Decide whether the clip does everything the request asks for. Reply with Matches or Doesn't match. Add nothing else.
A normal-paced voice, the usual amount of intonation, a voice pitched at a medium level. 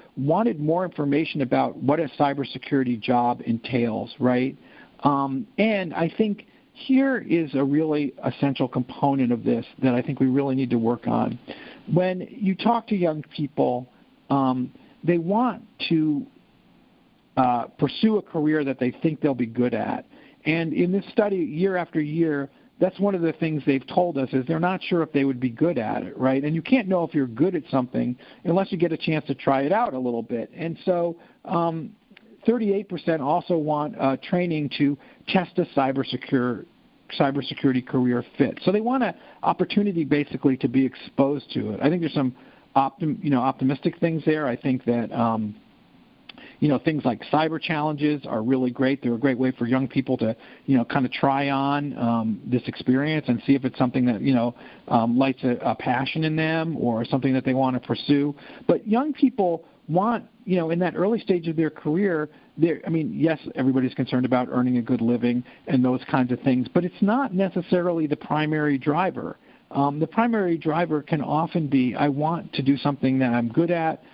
Matches